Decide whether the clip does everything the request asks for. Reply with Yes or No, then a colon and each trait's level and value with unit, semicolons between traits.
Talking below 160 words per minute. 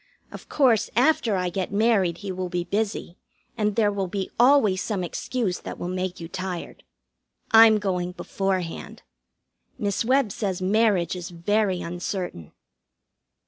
Yes: average, 140 wpm